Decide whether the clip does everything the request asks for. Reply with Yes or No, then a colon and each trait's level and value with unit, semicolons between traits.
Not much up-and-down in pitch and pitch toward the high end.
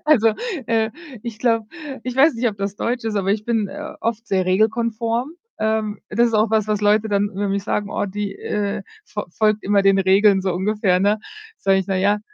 Yes: narrow, 2.2 semitones; high, 210 Hz